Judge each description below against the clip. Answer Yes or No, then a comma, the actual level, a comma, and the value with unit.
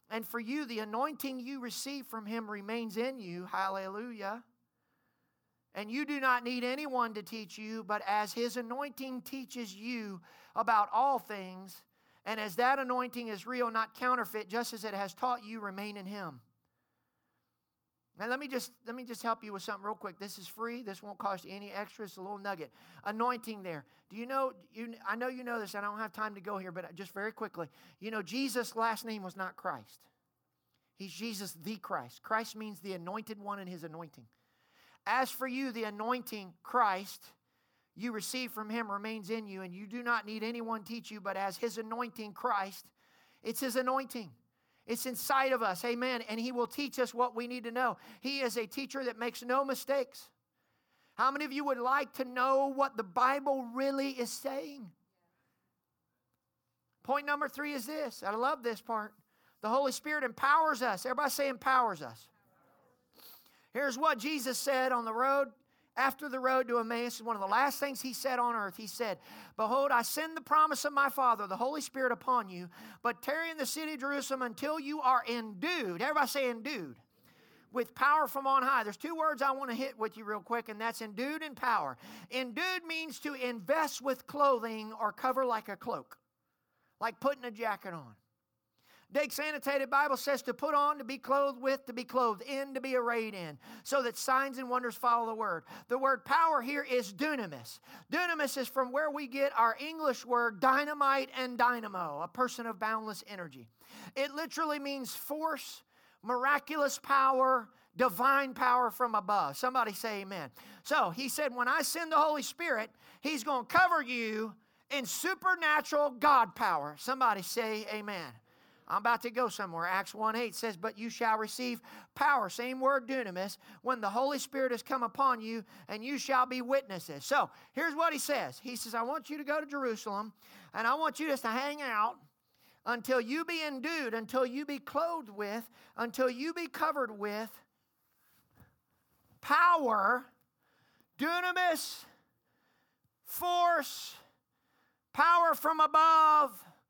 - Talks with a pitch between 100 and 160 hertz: No, high, 245 Hz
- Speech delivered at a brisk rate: No, average, 180 wpm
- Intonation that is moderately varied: Yes, average, 4.1 semitones